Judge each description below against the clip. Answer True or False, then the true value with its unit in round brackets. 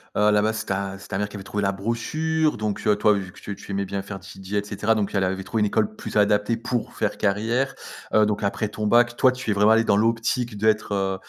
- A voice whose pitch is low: True (105 Hz)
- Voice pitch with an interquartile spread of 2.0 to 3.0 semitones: True (2.4 semitones)